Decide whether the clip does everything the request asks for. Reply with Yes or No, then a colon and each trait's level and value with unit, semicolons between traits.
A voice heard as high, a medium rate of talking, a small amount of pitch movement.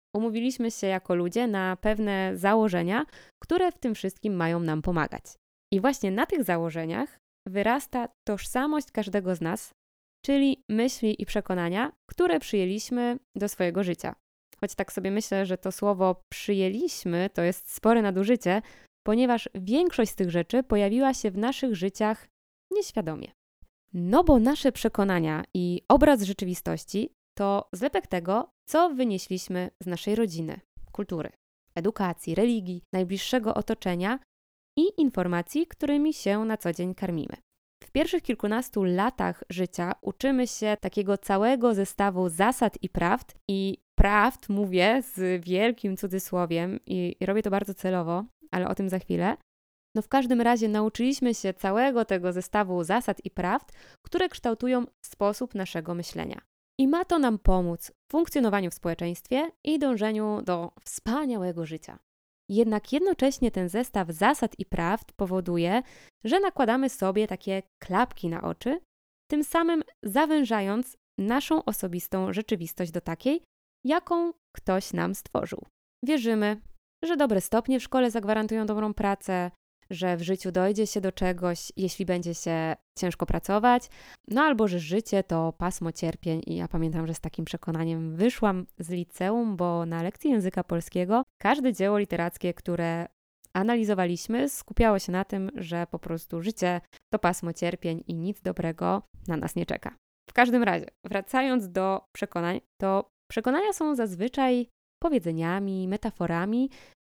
No: high, 205 Hz; average, 140 wpm; average, 5.1 semitones